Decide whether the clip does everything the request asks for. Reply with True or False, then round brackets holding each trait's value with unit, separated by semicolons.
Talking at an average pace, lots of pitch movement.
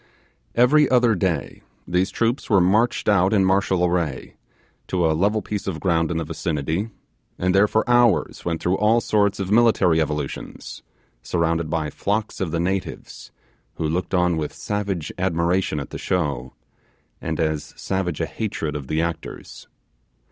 False (160 wpm; 4.0 semitones)